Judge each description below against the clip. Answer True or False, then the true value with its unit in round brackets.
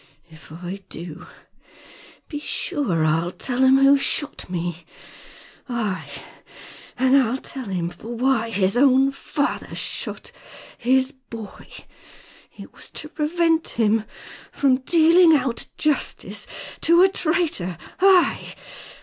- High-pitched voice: True (260 Hz)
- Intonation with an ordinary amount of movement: False (7.1 semitones)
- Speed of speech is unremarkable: False (115 wpm)